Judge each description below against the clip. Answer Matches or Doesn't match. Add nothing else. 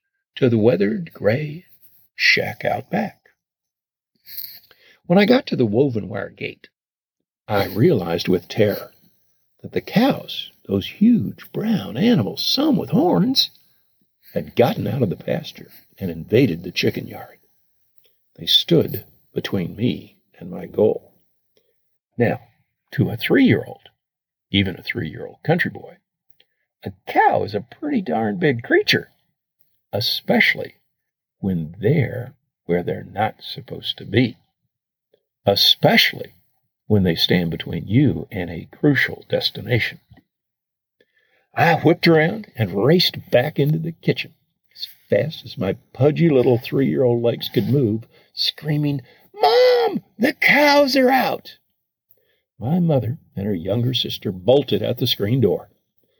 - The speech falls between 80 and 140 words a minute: Matches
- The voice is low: Doesn't match